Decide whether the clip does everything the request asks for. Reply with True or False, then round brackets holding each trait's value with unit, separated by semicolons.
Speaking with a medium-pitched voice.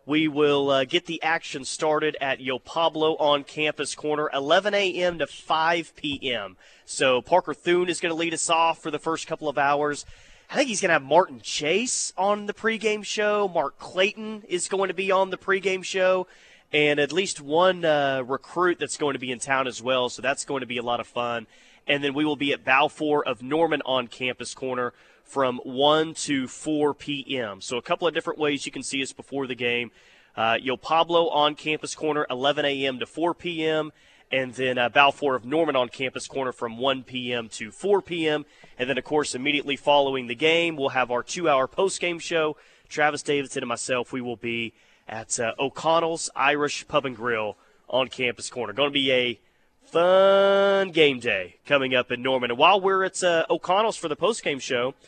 True (145 Hz)